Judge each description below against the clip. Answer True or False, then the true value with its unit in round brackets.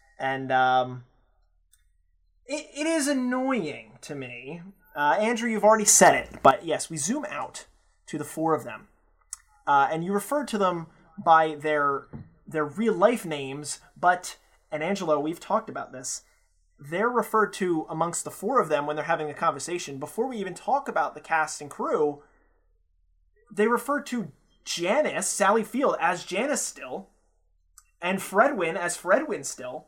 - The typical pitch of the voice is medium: True (160 Hz)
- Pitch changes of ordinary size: False (7.1 semitones)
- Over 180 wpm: False (160 wpm)